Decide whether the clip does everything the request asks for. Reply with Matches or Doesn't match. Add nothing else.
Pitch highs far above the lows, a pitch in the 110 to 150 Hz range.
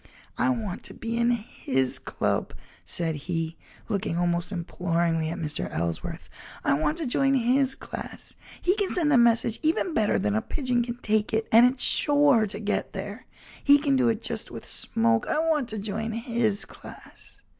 Doesn't match